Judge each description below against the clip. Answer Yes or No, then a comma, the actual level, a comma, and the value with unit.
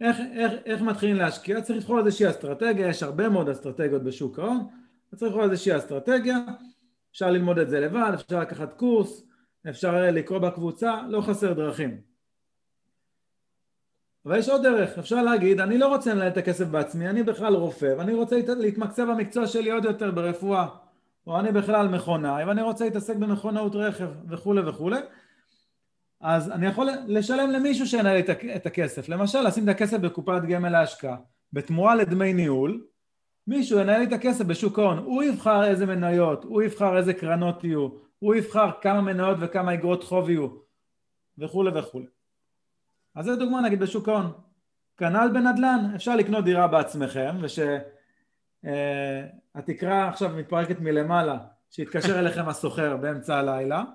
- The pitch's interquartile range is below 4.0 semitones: No, average, 4.8 semitones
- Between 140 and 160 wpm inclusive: Yes, fast, 150 wpm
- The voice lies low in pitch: No, high, 190 Hz